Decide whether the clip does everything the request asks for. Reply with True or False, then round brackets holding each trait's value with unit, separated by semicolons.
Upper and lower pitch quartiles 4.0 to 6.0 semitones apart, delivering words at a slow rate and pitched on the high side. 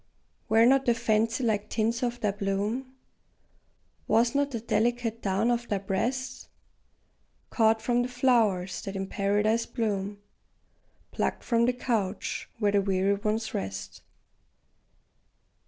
False (3.1 semitones; 130 wpm; 220 Hz)